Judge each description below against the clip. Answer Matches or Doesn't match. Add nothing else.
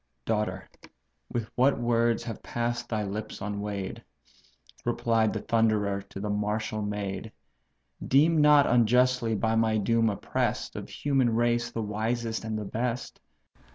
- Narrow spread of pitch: Matches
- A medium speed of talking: Doesn't match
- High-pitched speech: Doesn't match